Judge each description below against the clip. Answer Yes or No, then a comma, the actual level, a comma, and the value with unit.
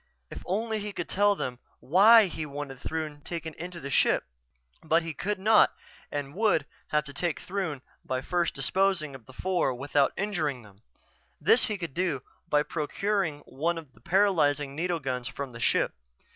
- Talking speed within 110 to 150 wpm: No, average, 175 wpm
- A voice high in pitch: No, medium, 160 Hz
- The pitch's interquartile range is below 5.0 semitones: No, average, 5.3 semitones